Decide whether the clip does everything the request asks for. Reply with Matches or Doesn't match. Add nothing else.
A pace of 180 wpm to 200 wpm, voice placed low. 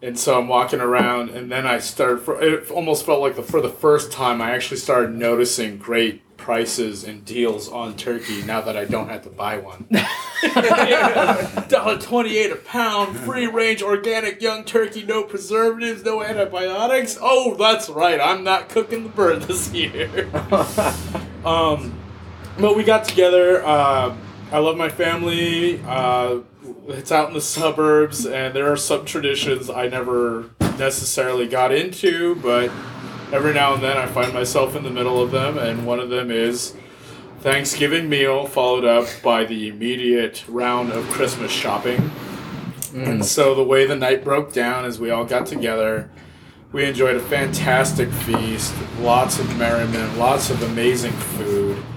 Doesn't match